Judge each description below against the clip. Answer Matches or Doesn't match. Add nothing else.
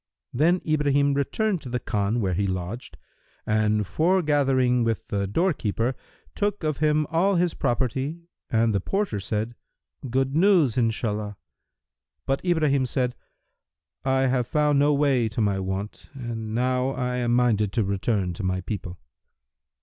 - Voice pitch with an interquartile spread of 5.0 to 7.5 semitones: Matches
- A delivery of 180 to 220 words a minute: Doesn't match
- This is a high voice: Doesn't match